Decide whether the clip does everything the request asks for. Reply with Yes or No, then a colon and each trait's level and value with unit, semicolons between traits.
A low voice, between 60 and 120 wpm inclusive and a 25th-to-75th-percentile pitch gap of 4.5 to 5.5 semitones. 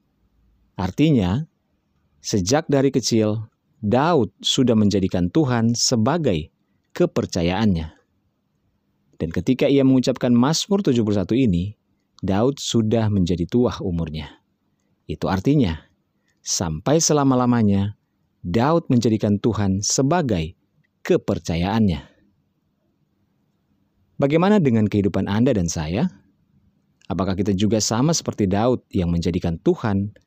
Yes: low, 105 Hz; average, 90 wpm; average, 5.1 semitones